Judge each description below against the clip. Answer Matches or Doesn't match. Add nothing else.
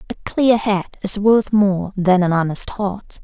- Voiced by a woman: Matches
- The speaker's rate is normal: Matches